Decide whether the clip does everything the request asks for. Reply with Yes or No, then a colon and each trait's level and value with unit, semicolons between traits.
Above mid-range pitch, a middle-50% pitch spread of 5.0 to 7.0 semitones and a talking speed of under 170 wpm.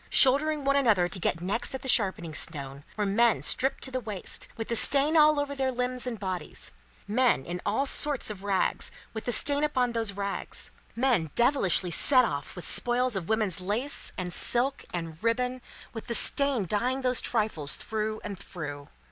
No: high, 230 Hz; wide, 5.4 semitones; average, 185 wpm